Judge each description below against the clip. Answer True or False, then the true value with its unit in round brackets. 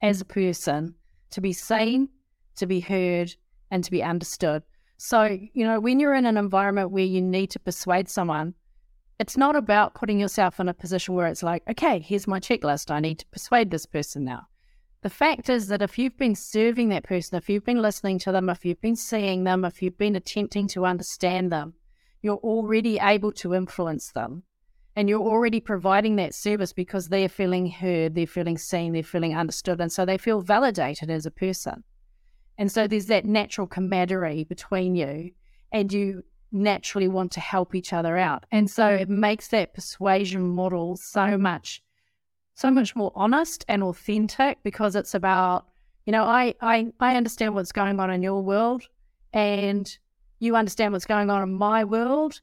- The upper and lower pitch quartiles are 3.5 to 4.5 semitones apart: False (3.0 semitones)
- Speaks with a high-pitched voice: True (195 Hz)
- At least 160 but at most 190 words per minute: True (185 wpm)